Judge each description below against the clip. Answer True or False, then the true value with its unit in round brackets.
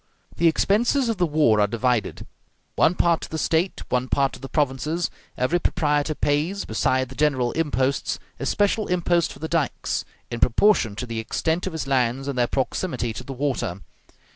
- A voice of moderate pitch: True (145 Hz)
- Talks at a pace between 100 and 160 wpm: False (185 wpm)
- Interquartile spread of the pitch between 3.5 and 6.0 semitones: True (5.1 semitones)